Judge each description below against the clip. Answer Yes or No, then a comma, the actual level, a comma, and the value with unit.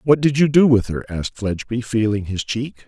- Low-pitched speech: Yes, low, 115 Hz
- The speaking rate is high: Yes, fast, 230 wpm